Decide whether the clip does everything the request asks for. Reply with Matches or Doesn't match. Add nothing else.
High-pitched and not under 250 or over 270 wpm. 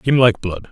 Doesn't match